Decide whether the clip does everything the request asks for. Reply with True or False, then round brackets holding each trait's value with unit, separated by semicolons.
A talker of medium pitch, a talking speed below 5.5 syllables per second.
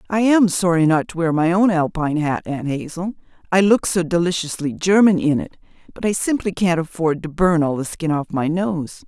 True (170 Hz; 5.2 syllables/s)